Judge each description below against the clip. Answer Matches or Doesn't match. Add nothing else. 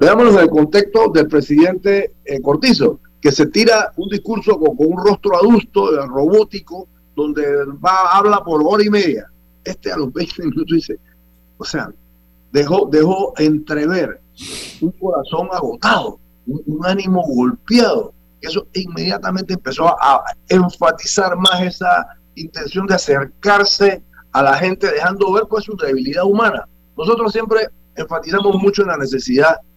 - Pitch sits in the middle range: Matches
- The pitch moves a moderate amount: Doesn't match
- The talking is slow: Doesn't match